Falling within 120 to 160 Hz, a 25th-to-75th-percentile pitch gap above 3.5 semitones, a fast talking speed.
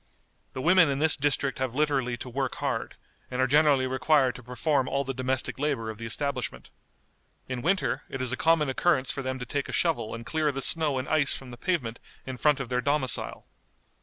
No: low, 135 Hz; average, 2.8 semitones; fast, 215 wpm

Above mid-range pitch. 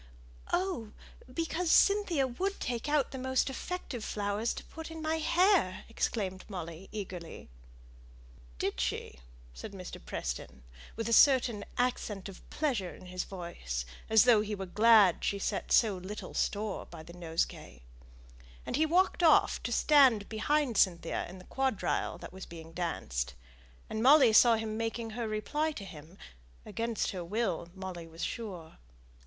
Yes: high, 215 Hz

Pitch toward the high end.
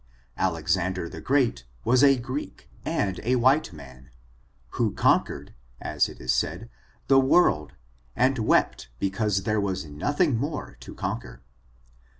No: low, 105 Hz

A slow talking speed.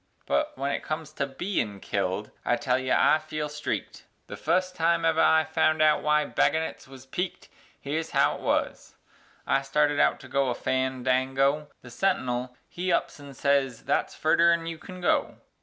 No: average, 190 wpm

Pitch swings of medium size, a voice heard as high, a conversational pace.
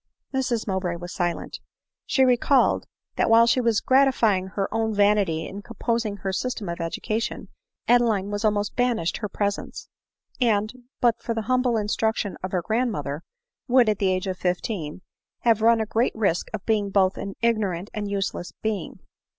Yes: average, 3.4 semitones; high, 210 Hz; average, 175 wpm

